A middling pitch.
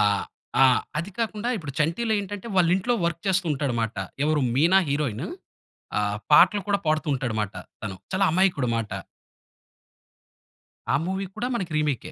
Yes: medium, 155 Hz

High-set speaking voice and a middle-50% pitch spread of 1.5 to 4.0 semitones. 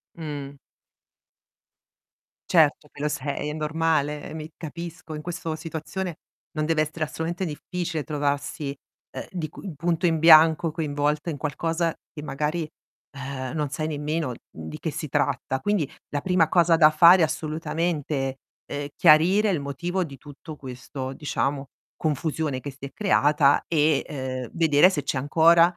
No: medium, 155 Hz; narrow, 2.5 semitones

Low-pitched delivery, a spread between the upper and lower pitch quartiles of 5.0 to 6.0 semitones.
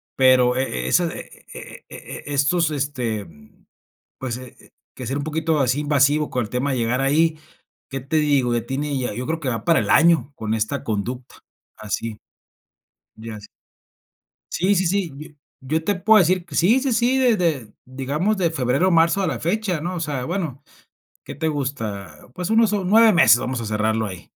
No: medium, 145 Hz; wide, 5.4 semitones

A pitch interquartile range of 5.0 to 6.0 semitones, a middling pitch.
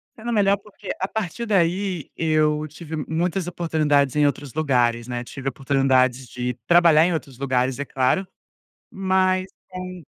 Yes: wide, 5.5 semitones; medium, 155 Hz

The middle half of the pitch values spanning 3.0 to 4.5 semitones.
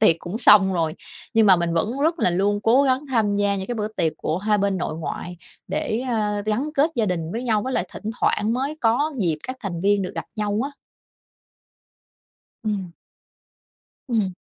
Yes: average, 3.7 semitones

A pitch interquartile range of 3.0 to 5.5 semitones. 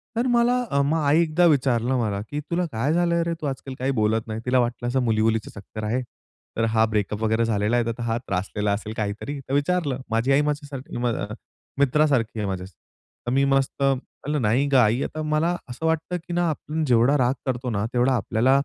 Yes: average, 4.9 semitones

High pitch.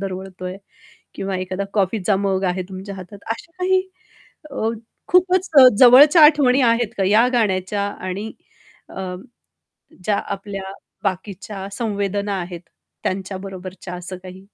Yes: high, 195 Hz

